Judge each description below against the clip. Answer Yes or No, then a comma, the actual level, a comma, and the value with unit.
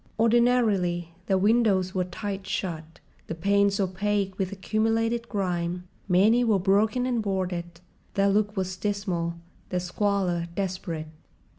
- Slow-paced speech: Yes, slow, 120 wpm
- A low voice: No, high, 195 Hz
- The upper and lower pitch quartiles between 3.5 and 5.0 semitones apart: No, average, 2.8 semitones